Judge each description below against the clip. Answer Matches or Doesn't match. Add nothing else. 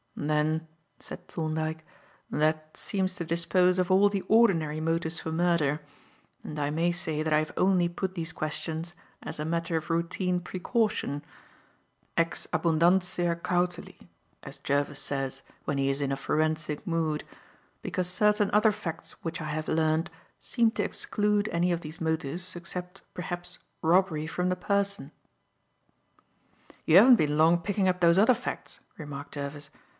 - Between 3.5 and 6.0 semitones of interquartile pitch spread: Doesn't match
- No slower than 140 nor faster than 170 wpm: Matches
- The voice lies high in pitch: Doesn't match